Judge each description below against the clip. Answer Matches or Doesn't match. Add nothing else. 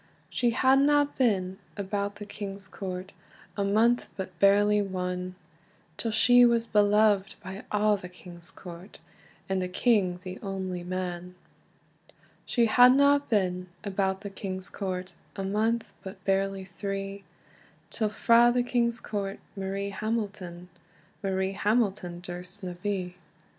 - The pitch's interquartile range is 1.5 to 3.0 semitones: Matches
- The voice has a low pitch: Doesn't match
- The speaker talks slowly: Matches